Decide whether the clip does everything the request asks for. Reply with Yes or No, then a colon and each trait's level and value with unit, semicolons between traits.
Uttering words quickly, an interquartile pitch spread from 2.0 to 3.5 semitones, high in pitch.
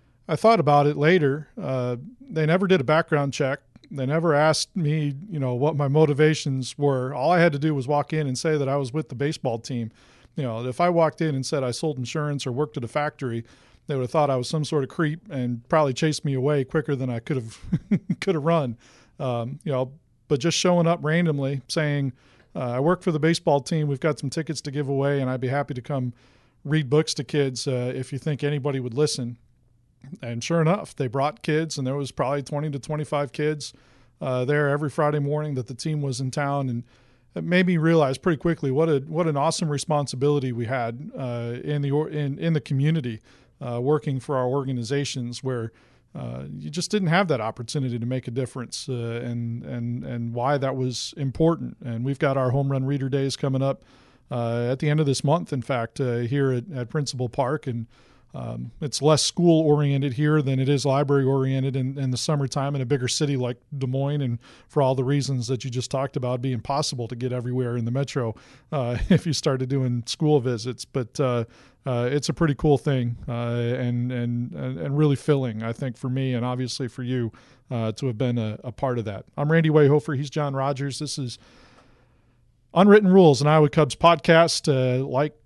No: fast, 220 wpm; average, 3.2 semitones; medium, 140 Hz